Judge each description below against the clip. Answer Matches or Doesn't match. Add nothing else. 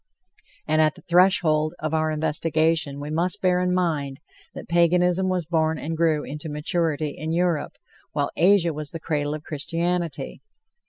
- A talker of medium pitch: Matches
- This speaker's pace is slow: Doesn't match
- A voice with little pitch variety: Matches